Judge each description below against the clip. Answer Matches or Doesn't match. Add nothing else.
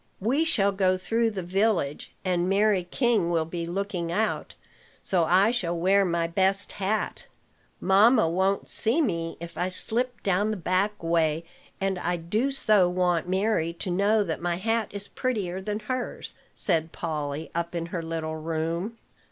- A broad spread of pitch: Doesn't match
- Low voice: Doesn't match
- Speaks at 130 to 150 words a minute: Doesn't match